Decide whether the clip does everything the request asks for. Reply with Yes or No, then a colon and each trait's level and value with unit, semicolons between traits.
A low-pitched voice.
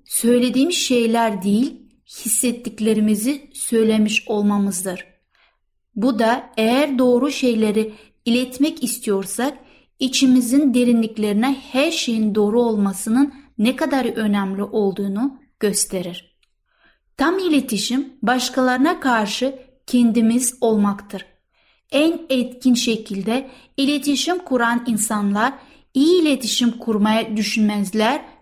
No: high, 240 Hz